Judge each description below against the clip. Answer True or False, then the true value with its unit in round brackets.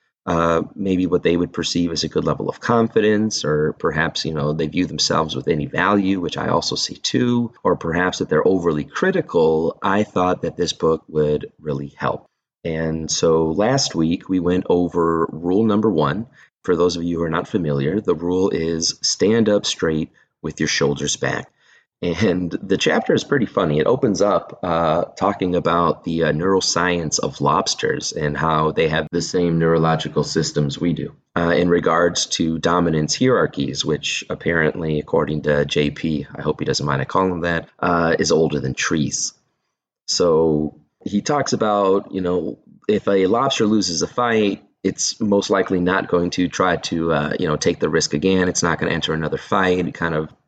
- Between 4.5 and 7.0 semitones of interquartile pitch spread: False (3.2 semitones)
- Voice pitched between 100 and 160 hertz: False (85 Hz)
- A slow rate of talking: False (190 wpm)